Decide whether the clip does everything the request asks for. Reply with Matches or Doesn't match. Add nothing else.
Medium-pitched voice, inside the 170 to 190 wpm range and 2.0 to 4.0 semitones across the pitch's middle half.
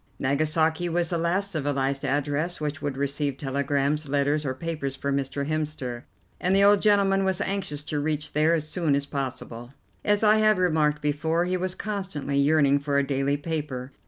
Matches